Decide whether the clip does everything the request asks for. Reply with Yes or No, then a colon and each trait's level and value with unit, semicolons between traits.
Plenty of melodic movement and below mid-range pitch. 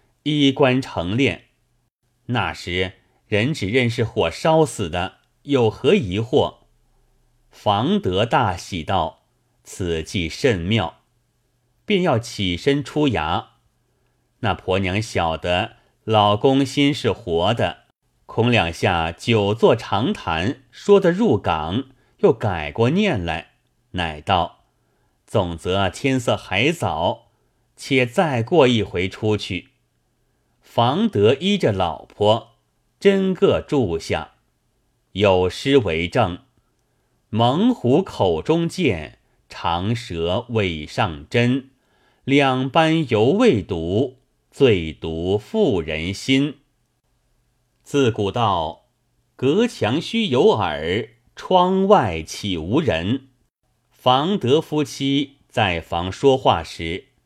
Yes: wide, 6.2 semitones; low, 120 Hz